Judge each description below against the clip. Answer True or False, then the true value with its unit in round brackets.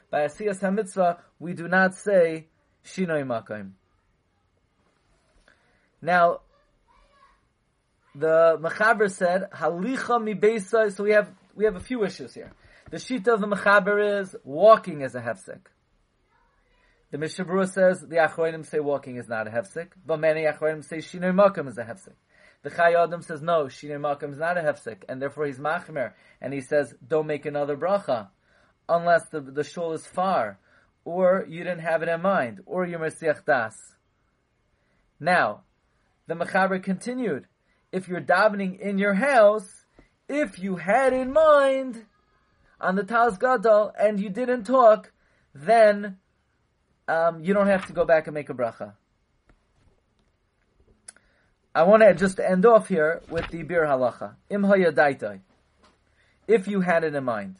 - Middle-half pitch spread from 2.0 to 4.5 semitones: False (5.3 semitones)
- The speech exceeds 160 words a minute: False (145 wpm)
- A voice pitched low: False (170 Hz)